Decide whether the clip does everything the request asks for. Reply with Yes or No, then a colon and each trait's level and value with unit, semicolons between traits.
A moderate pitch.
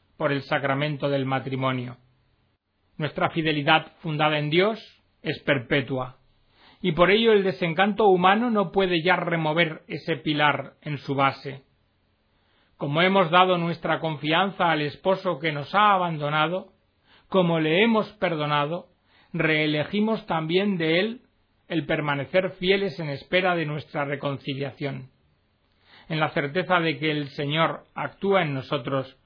Yes: medium, 155 Hz